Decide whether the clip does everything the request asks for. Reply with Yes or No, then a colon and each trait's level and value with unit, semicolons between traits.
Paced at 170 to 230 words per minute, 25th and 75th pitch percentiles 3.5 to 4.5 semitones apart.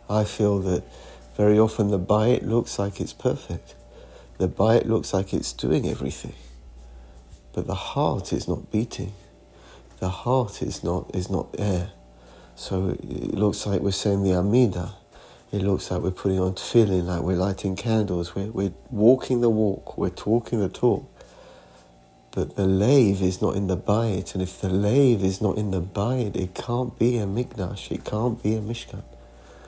No: average, 175 wpm; average, 3.0 semitones